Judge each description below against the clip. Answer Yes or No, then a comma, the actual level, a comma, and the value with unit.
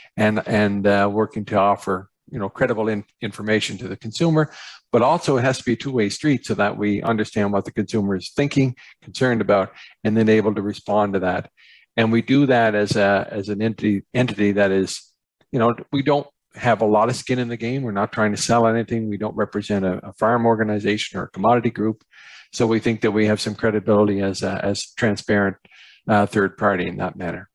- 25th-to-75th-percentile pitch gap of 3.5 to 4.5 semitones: No, narrow, 2.5 semitones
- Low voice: Yes, low, 110 Hz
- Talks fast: Yes, fast, 220 wpm